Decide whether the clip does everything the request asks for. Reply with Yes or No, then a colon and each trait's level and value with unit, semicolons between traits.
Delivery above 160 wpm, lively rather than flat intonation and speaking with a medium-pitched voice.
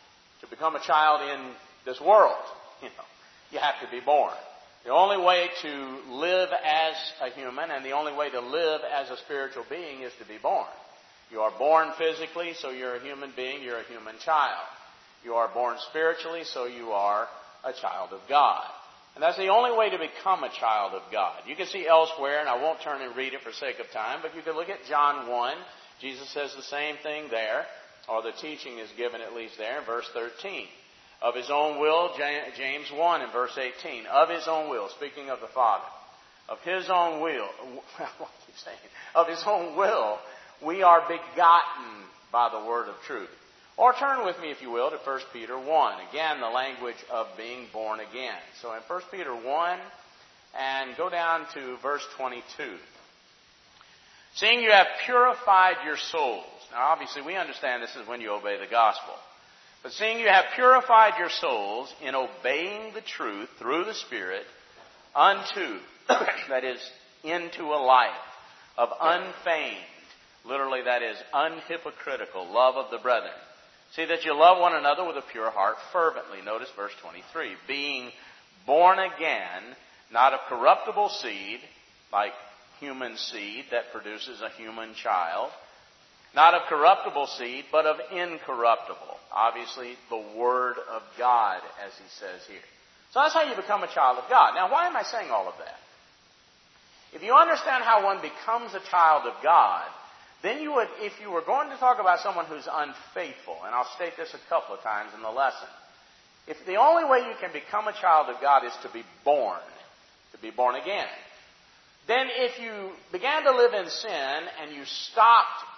Yes: average, 180 wpm; wide, 6.4 semitones; medium, 155 Hz